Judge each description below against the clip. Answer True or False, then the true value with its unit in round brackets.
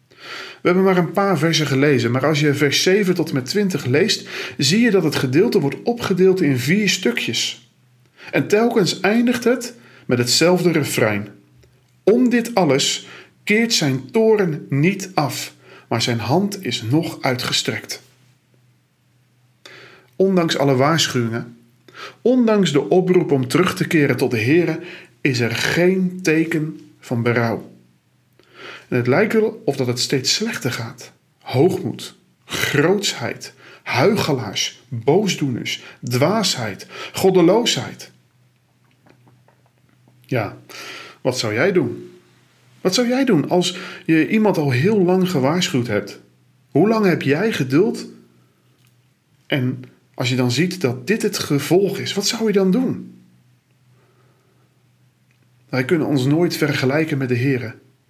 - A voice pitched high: False (140 Hz)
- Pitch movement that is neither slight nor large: False (6.4 semitones)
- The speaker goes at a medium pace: False (130 wpm)